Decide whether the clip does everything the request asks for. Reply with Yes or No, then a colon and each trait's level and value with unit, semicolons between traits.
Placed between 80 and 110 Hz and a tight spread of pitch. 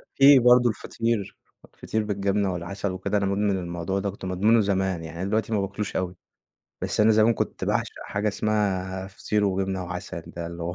Yes: low, 100 Hz; narrow, 2.3 semitones